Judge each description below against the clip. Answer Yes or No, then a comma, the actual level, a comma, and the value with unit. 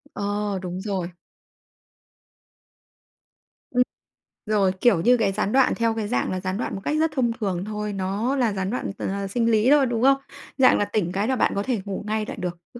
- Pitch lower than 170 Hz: No, high, 210 Hz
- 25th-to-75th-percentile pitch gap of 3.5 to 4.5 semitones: Yes, average, 3.9 semitones